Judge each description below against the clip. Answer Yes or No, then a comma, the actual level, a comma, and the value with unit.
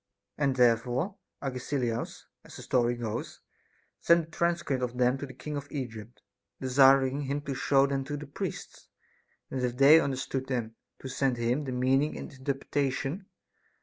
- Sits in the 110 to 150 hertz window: Yes, low, 135 Hz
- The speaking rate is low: No, average, 160 wpm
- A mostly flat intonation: Yes, narrow, 2.3 semitones